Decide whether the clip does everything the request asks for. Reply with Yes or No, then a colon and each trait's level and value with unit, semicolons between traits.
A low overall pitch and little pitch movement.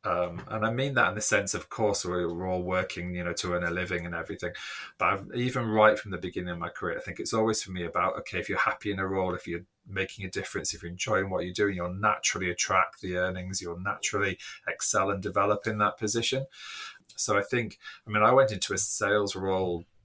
No: very low, 95 Hz; average, 3.0 semitones